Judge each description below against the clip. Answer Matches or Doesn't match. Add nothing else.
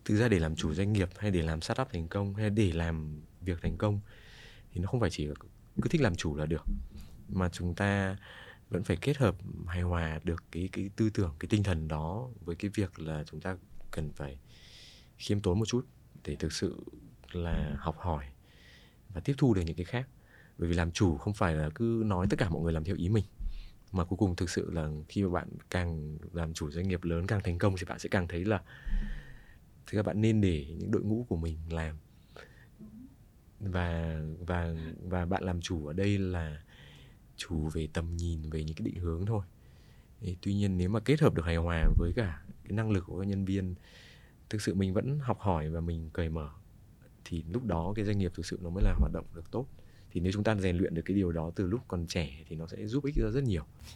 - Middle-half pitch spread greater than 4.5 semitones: Doesn't match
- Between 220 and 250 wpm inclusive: Matches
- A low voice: Matches